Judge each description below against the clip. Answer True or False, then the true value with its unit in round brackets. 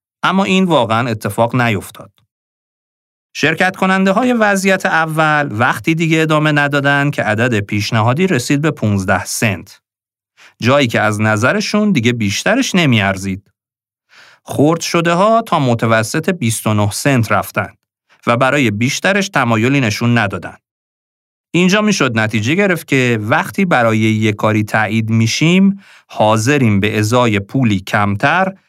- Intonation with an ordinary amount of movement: False (6.9 semitones)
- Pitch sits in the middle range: False (125 Hz)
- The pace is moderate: True (120 wpm)